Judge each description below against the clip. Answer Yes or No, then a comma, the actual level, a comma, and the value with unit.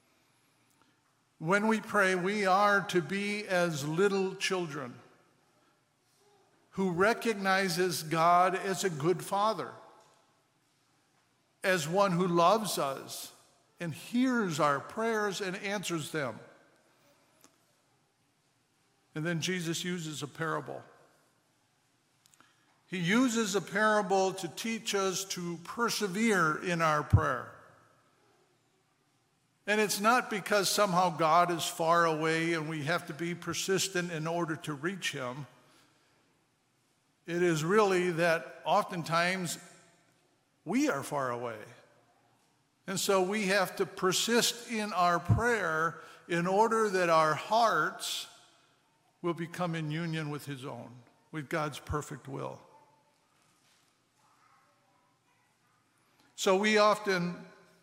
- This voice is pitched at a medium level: Yes, medium, 175 Hz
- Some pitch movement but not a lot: Yes, average, 4.1 semitones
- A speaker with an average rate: No, slow, 110 wpm